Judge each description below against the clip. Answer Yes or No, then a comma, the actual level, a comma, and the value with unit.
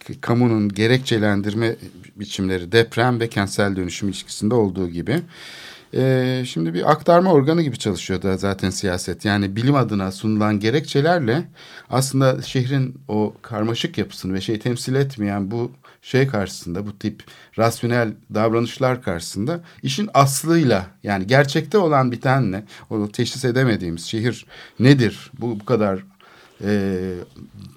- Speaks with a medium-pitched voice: No, low, 115 Hz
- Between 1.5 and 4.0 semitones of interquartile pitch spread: No, average, 4.4 semitones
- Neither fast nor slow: Yes, average, 125 wpm